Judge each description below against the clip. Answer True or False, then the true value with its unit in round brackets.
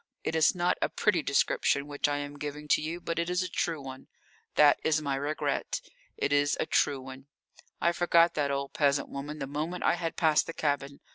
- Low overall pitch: False (150 Hz)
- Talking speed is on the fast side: True (215 wpm)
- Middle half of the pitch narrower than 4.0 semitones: True (2.8 semitones)